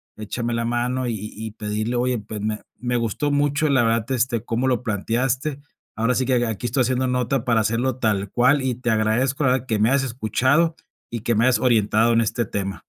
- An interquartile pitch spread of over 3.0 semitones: No, average, 2.7 semitones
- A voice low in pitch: Yes, low, 120 Hz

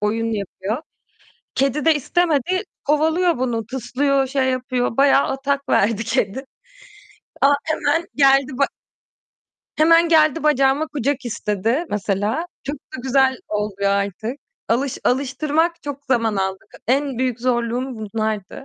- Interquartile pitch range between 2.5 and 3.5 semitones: No, average, 4.1 semitones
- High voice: Yes, very high, 265 Hz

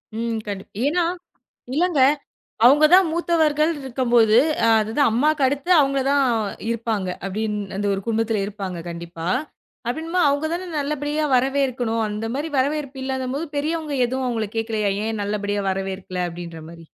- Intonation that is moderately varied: No, wide, 5.8 semitones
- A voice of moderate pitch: No, high, 245 Hz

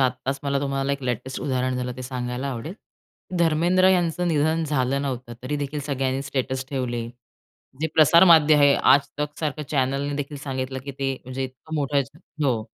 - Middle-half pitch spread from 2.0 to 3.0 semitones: Yes, narrow, 2.4 semitones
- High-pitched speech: No, medium, 140 Hz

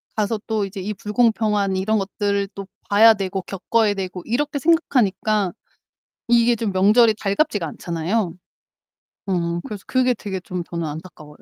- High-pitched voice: Yes, high, 205 Hz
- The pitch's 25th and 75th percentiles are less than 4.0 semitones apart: Yes, average, 3.2 semitones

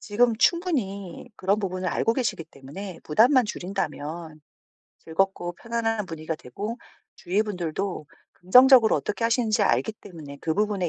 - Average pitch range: Yes, average, 4.8 semitones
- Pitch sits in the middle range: No, high, 195 Hz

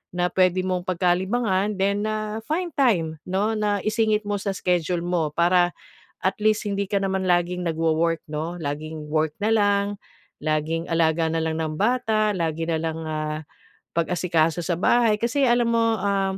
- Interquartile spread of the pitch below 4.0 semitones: No, average, 4.3 semitones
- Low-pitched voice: No, medium, 185 Hz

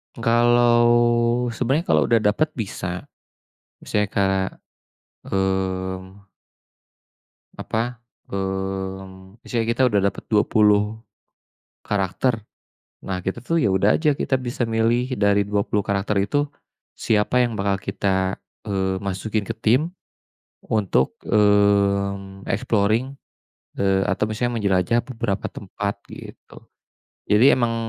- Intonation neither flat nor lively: Yes, average, 3.2 semitones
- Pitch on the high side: No, low, 105 Hz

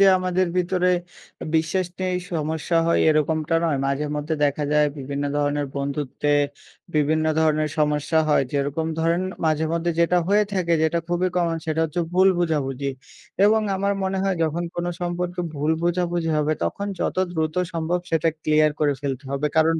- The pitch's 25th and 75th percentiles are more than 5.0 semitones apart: No, average, 2.8 semitones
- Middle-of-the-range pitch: Yes, medium, 160 Hz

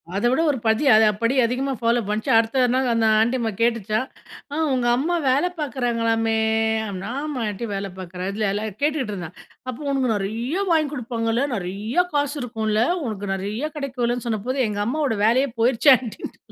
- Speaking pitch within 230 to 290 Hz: Yes, high, 235 Hz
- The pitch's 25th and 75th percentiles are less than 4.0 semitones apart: Yes, average, 3.4 semitones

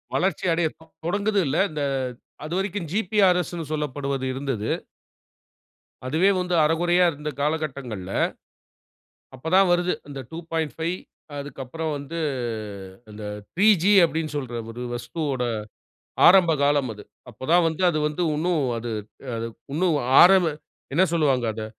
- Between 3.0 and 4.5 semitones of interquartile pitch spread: Yes, average, 4.2 semitones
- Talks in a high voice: No, medium, 160 Hz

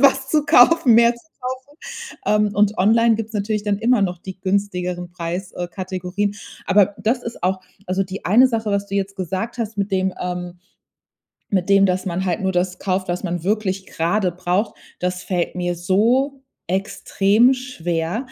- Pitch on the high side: Yes, high, 195 Hz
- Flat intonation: No, average, 3.3 semitones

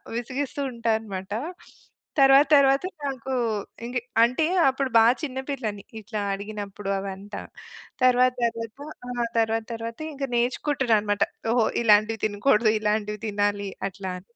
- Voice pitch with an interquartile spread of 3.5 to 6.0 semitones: Yes, average, 3.8 semitones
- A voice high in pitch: Yes, high, 225 Hz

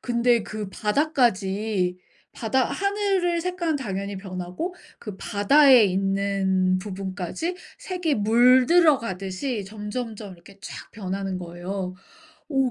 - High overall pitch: Yes, high, 210 Hz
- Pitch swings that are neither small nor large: No, wide, 5.8 semitones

